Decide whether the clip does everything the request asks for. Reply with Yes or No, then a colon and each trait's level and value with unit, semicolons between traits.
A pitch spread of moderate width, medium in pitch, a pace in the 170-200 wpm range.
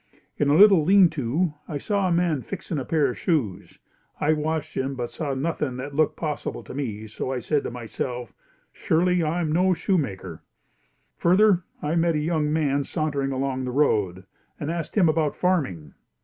Yes: average, 4.2 semitones; medium, 150 Hz; average, 175 wpm